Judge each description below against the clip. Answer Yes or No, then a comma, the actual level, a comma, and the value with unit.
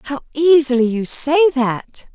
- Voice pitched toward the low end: No, very high, 255 Hz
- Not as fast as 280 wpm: Yes, average, 140 wpm